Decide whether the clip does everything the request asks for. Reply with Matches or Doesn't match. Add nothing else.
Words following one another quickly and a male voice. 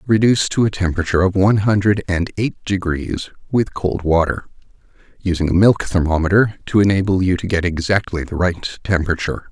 Doesn't match